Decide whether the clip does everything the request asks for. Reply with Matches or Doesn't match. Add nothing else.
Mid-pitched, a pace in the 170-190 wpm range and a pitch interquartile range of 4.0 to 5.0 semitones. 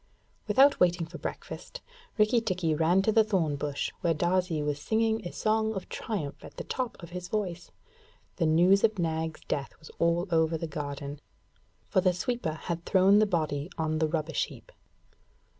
Matches